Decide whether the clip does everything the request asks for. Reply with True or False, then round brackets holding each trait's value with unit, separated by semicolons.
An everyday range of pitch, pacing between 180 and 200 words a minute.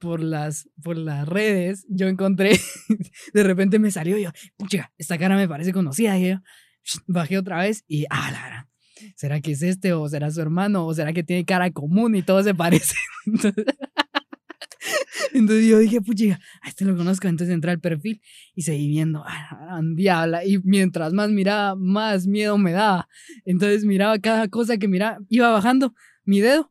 True (3.8 semitones; 185 wpm)